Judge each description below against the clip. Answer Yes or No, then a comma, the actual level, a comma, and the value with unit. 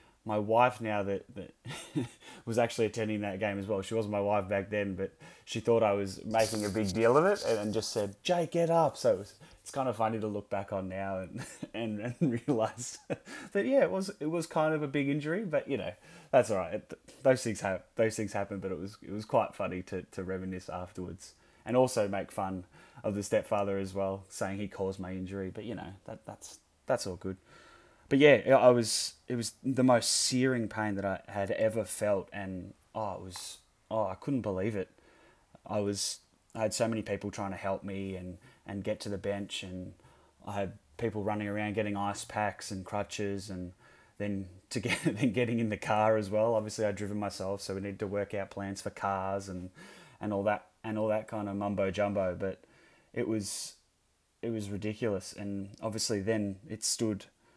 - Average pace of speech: No, fast, 215 wpm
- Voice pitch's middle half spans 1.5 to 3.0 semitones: Yes, narrow, 2.4 semitones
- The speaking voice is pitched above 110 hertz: No, low, 105 Hz